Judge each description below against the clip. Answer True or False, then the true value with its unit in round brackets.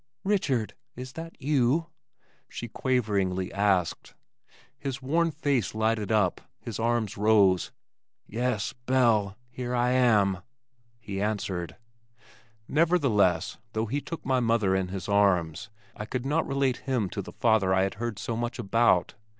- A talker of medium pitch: False (115 Hz)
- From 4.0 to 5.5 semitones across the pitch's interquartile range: True (4.6 semitones)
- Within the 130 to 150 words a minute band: True (140 wpm)